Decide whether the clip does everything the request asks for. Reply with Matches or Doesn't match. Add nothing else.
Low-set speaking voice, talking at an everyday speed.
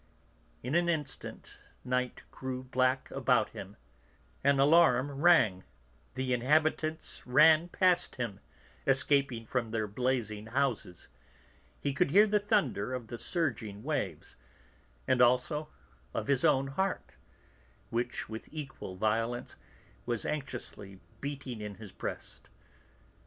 Doesn't match